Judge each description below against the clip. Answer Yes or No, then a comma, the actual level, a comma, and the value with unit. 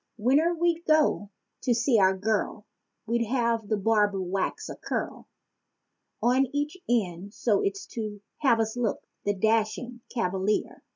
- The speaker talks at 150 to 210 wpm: No, slow, 135 wpm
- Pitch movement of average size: Yes, average, 3.3 semitones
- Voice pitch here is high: Yes, high, 225 Hz